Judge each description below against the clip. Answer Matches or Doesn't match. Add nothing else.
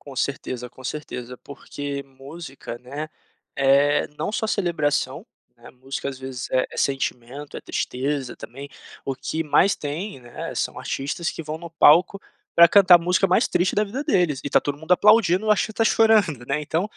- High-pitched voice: Doesn't match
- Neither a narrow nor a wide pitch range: Matches